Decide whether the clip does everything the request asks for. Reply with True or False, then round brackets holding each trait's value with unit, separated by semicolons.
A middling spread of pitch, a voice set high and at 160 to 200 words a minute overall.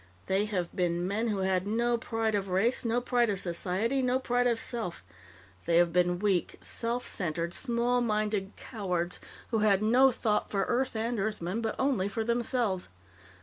True (4.1 semitones; 215 Hz; 175 wpm)